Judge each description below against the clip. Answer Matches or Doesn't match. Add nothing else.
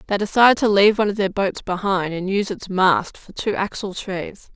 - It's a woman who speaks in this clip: Matches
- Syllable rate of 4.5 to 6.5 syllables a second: Matches